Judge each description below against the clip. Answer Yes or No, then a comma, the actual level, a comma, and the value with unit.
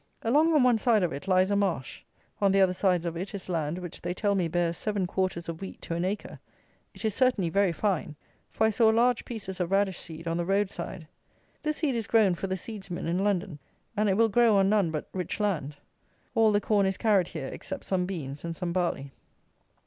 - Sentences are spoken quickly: Yes, fast, 230 wpm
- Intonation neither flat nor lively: Yes, average, 3.5 semitones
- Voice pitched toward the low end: No, high, 190 Hz